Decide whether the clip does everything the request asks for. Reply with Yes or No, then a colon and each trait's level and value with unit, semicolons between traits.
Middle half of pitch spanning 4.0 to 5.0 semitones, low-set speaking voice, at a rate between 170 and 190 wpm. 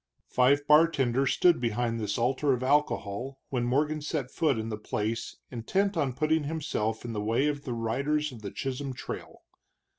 Yes: average, 4.4 semitones; low, 130 Hz; average, 175 wpm